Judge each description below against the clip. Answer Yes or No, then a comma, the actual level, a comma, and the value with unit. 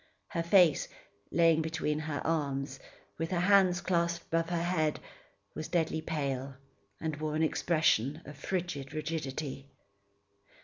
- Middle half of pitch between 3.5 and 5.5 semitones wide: No, narrow, 2.5 semitones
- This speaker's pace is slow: Yes, slow, 130 wpm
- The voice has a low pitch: No, medium, 160 Hz